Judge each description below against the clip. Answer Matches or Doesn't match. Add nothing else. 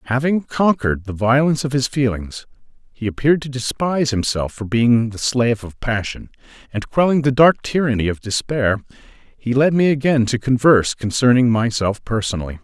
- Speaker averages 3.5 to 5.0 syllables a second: Doesn't match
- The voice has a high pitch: Doesn't match